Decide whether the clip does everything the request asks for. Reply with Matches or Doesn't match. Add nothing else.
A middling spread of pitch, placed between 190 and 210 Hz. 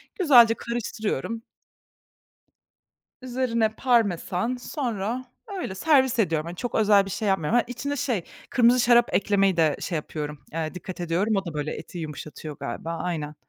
Doesn't match